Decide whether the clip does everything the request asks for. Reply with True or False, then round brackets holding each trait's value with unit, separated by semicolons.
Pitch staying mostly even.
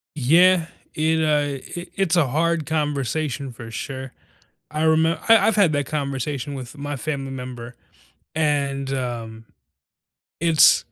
False (3.2 semitones)